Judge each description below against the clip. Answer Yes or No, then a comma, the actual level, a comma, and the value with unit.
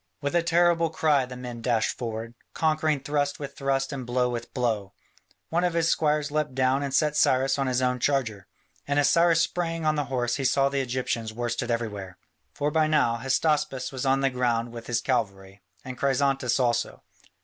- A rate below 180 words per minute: No, average, 195 wpm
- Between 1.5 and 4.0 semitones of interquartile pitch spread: Yes, average, 3.7 semitones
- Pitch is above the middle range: No, low, 135 Hz